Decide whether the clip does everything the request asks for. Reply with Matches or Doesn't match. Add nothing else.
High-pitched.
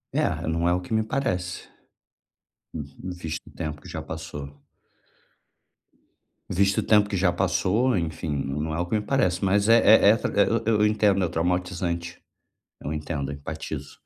Doesn't match